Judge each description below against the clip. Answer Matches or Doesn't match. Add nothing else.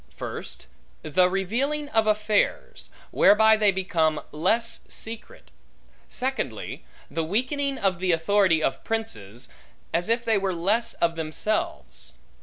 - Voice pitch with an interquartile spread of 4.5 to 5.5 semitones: Matches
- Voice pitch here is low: Doesn't match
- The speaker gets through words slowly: Matches